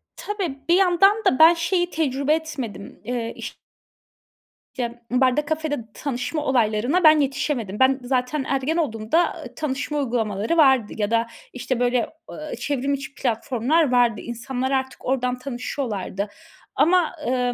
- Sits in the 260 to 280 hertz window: Yes, very high, 265 Hz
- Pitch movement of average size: Yes, average, 4.0 semitones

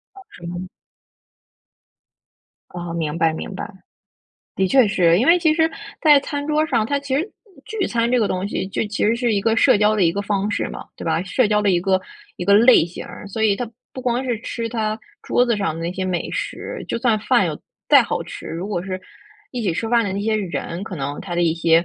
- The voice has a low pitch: No, high, 205 Hz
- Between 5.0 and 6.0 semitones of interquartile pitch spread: Yes, wide, 5.4 semitones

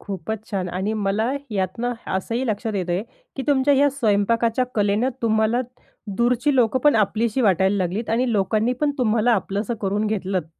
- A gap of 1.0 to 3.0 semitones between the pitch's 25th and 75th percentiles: No, average, 3.5 semitones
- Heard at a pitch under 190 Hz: No, high, 220 Hz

